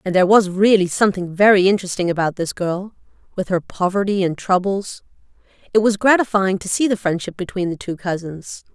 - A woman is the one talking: Yes, female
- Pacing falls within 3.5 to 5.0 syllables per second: No, 5.8 syllables/s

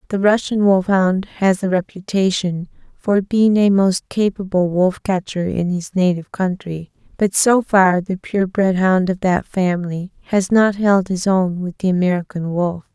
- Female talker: Yes, female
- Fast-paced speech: No, average, 165 wpm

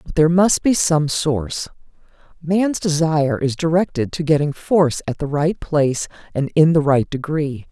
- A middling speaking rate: Yes, average, 170 wpm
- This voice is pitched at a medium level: Yes, medium, 155 Hz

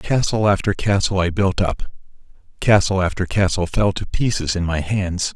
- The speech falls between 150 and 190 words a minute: Yes, average, 170 wpm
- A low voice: Yes, very low, 95 Hz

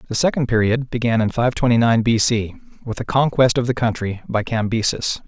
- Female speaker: No, male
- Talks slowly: No, fast, 205 wpm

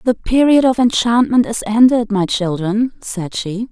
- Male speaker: No, female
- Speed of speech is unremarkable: Yes, average, 160 wpm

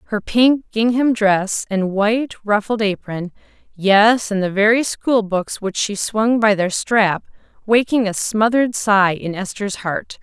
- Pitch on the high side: Yes, high, 210 Hz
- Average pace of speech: Yes, average, 155 wpm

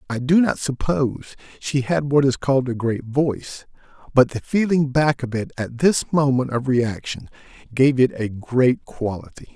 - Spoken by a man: Yes, male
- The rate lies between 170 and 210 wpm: Yes, average, 175 wpm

